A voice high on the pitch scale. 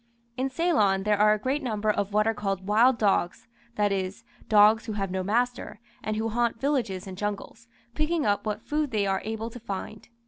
Yes: high, 215 Hz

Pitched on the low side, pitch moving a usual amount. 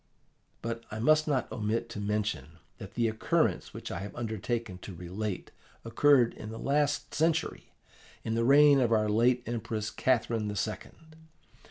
Yes: low, 115 Hz; average, 3.3 semitones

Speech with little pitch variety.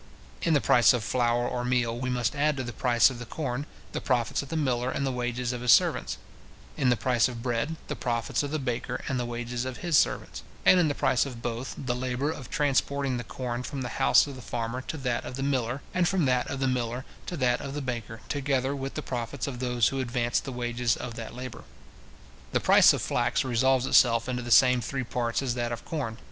Yes: narrow, 2.1 semitones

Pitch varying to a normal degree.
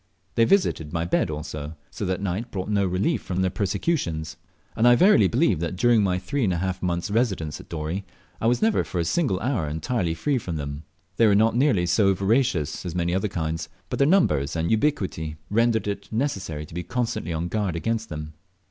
No: wide, 5.8 semitones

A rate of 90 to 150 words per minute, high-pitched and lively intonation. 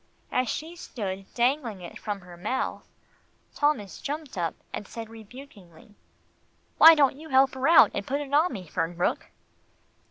Yes: average, 145 wpm; high, 240 Hz; wide, 6.6 semitones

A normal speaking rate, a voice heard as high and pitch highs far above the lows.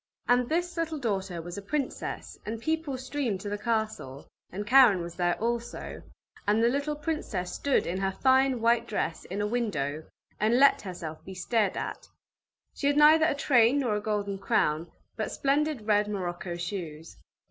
Yes: average, 175 wpm; high, 220 Hz; wide, 6.4 semitones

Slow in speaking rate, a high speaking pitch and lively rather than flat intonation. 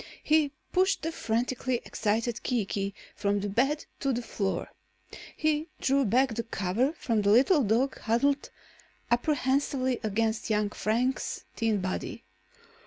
No: slow, 130 wpm; high, 240 Hz; average, 4.3 semitones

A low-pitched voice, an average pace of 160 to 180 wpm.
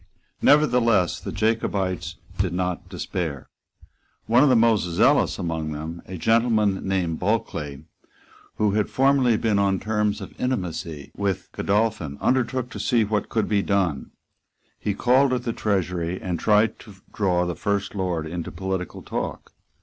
No: low, 100 Hz; average, 150 wpm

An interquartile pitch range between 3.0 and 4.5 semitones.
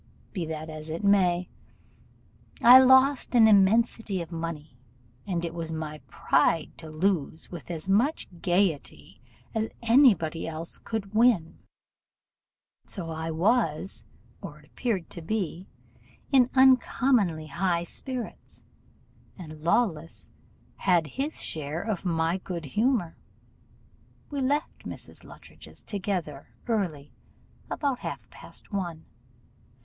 No: wide, 5.6 semitones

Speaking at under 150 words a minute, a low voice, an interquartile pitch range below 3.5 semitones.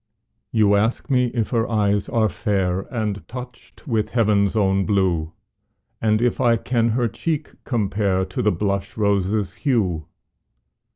Yes: average, 140 wpm; low, 105 Hz; average, 3.0 semitones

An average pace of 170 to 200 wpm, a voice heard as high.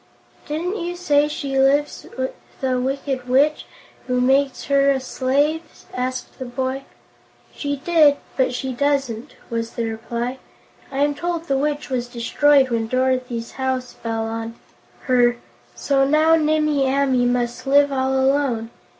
No: average, 145 wpm; very high, 265 Hz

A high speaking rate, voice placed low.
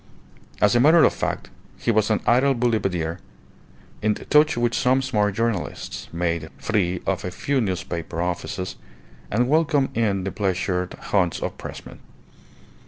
No: average, 145 wpm; low, 105 Hz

